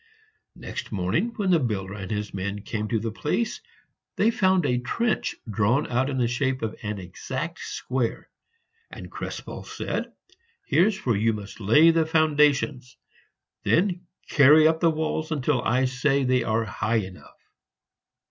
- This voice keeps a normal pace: Yes, average, 155 wpm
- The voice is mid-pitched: No, low, 130 Hz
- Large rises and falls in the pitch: Yes, wide, 6.4 semitones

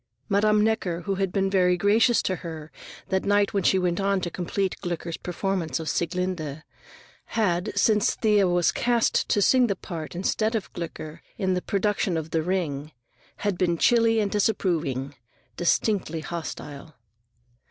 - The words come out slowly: No, average, 155 wpm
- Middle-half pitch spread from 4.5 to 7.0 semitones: No, average, 3.4 semitones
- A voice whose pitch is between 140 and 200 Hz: Yes, medium, 185 Hz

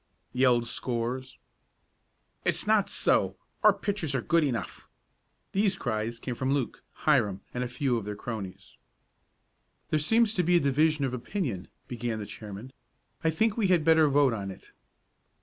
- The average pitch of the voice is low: Yes, low, 130 Hz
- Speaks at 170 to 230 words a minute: No, average, 160 wpm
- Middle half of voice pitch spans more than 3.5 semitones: Yes, wide, 5.6 semitones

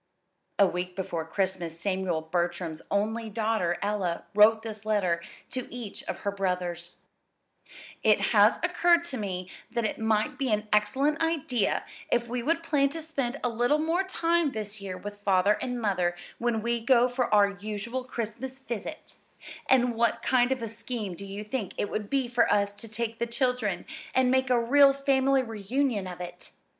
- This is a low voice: No, high, 225 Hz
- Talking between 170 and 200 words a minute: Yes, average, 175 wpm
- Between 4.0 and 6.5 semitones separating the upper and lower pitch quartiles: Yes, average, 4.3 semitones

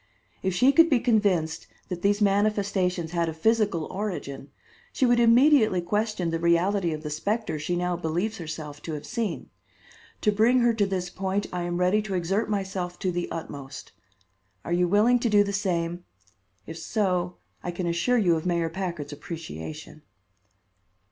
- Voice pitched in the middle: Yes, medium, 180 Hz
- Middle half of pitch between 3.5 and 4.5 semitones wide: Yes, average, 3.8 semitones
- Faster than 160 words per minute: Yes, average, 170 wpm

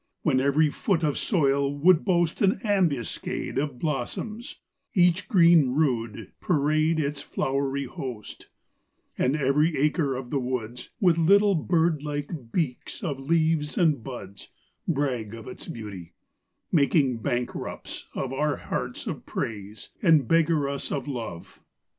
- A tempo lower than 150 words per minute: Yes, slow, 135 wpm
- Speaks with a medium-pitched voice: Yes, medium, 145 Hz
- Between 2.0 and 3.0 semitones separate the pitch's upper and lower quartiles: No, average, 4.3 semitones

